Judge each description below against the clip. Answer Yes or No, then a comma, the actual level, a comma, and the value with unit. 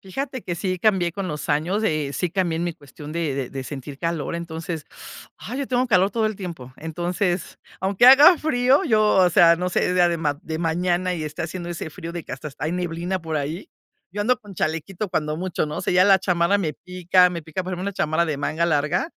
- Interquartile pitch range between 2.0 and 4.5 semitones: Yes, average, 3.1 semitones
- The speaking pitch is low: No, medium, 175 Hz